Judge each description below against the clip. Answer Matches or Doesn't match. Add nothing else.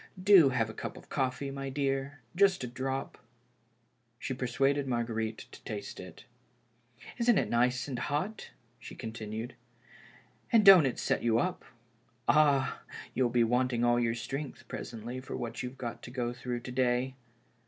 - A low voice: Matches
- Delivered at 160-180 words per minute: Matches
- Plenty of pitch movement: Doesn't match